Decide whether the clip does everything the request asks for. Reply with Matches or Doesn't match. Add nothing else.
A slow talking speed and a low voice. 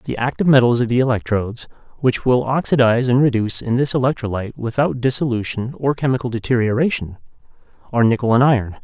Doesn't match